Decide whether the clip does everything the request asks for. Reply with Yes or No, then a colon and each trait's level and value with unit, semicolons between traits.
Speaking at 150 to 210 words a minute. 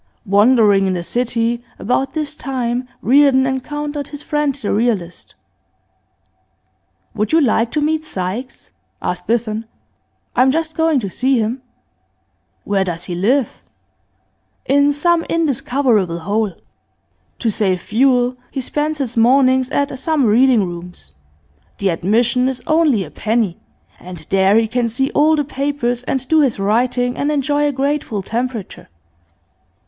No: average, 140 wpm